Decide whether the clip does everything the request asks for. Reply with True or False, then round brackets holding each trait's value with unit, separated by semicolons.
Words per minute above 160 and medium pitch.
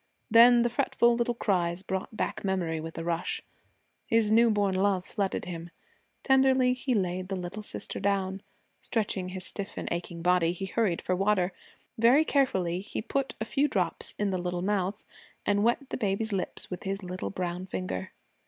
False (180 wpm; 195 Hz)